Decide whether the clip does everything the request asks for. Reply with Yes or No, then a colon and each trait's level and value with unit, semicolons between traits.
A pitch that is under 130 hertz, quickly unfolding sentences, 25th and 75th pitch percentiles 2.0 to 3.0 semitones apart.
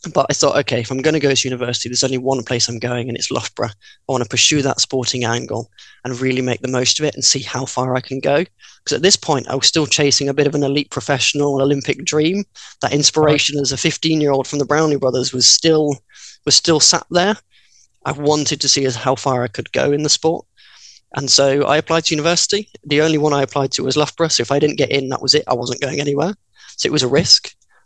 No: medium, 140 Hz; fast, 255 wpm; narrow, 2.6 semitones